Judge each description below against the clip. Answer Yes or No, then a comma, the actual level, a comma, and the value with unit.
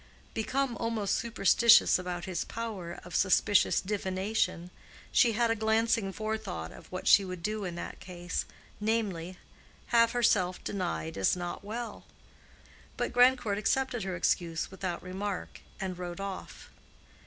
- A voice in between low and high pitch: No, high, 195 Hz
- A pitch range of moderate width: Yes, average, 3.8 semitones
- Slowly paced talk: Yes, slow, 130 wpm